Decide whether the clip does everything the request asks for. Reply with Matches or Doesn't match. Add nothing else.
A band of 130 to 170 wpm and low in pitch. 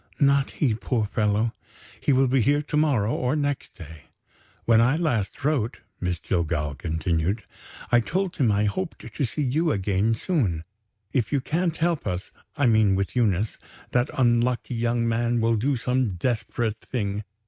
Matches